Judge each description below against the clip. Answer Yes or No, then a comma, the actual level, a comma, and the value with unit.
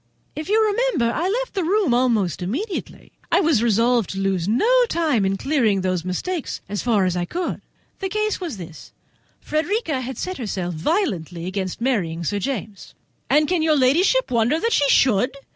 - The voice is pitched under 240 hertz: No, very high, 255 Hz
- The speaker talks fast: No, average, 175 wpm